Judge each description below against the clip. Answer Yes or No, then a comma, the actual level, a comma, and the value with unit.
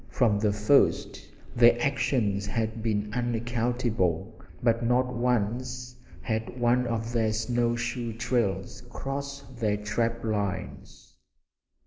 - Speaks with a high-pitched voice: No, low, 115 Hz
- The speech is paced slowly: Yes, slow, 110 wpm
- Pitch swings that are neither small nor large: No, narrow, 2.3 semitones